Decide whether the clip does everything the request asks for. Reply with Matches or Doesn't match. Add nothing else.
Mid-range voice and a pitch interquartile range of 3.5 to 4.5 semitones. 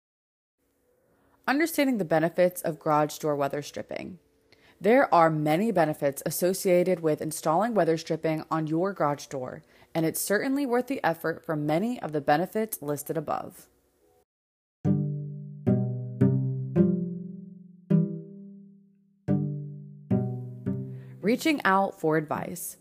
Matches